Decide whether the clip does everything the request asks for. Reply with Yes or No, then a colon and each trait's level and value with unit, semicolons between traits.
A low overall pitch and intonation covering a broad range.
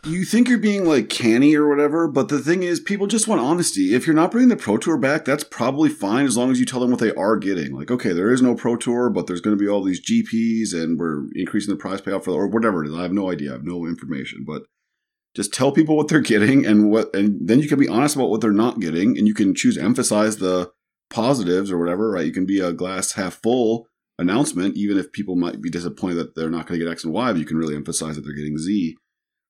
Yes: low, 110 Hz; wide, 8.5 semitones